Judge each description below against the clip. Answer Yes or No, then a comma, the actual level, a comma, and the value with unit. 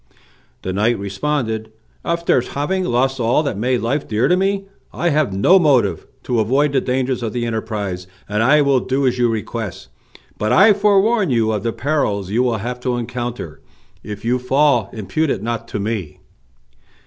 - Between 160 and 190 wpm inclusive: Yes, average, 180 wpm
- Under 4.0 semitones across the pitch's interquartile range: No, average, 4.6 semitones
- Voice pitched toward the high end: No, low, 120 Hz